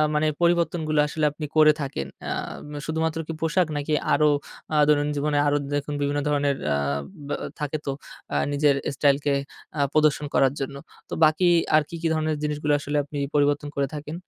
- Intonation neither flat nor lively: No, narrow, 1.3 semitones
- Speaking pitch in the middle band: Yes, medium, 150 Hz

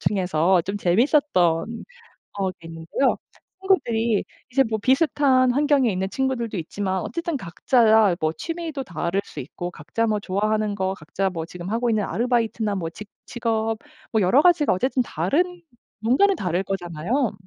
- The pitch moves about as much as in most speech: No, wide, 6.0 semitones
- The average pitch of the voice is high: Yes, high, 220 Hz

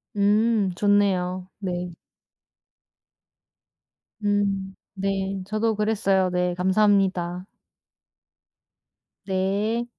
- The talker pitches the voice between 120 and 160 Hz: No, high, 195 Hz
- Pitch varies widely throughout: No, narrow, 1.8 semitones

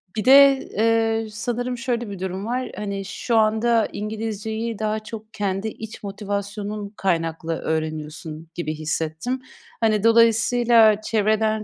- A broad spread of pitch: No, narrow, 2.5 semitones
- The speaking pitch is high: Yes, high, 215 Hz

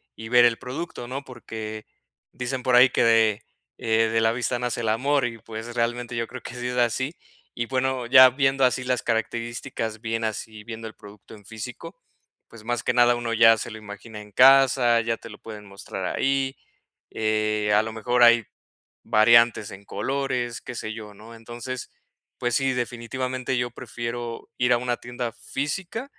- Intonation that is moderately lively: No, narrow, 2.0 semitones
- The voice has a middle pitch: No, low, 120 Hz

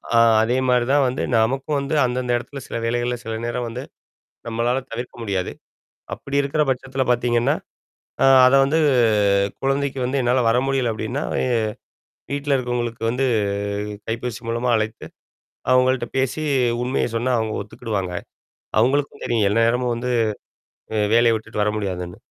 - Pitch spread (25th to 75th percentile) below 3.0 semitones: Yes, narrow, 2.5 semitones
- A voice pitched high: No, low, 125 Hz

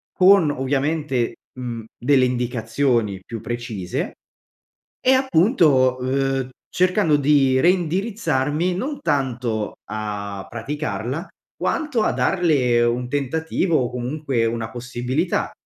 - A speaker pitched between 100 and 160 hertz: Yes, low, 135 Hz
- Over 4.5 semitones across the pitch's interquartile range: Yes, average, 5.1 semitones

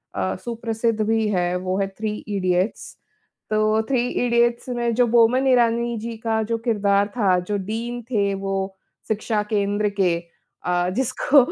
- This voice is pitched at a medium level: No, high, 215 Hz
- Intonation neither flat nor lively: Yes, average, 3.0 semitones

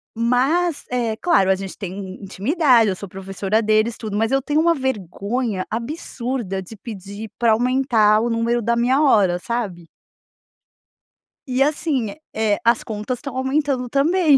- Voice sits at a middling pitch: No, high, 235 Hz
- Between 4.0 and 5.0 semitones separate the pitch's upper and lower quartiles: Yes, average, 4.4 semitones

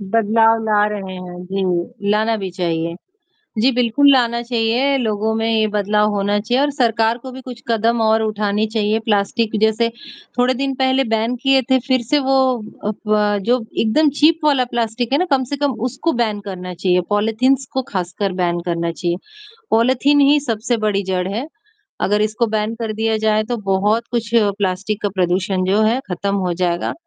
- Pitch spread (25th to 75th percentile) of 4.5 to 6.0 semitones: No, average, 3.4 semitones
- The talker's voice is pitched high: Yes, high, 220 Hz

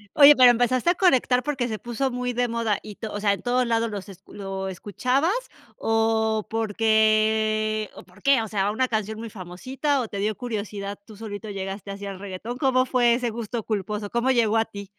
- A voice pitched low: No, high, 220 Hz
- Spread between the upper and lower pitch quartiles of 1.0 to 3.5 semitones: Yes, average, 3.1 semitones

